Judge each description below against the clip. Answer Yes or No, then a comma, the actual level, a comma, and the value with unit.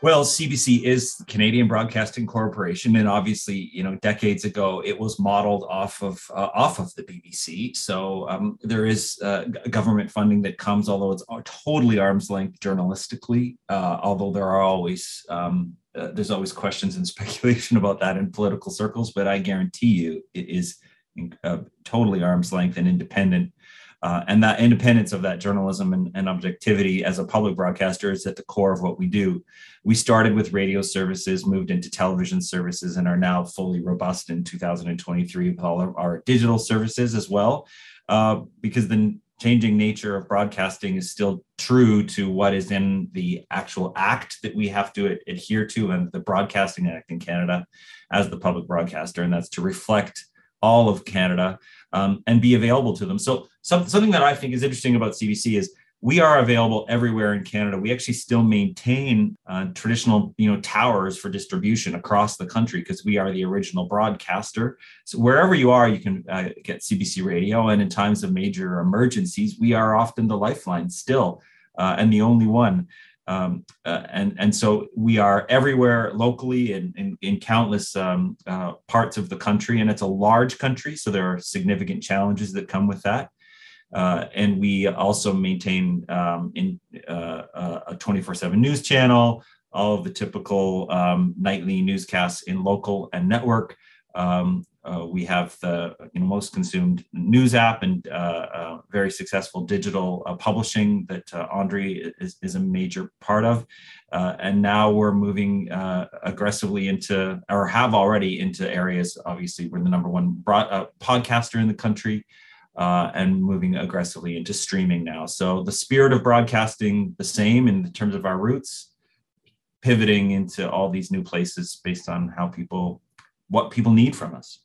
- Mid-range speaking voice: No, low, 110 Hz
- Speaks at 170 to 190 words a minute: Yes, average, 175 wpm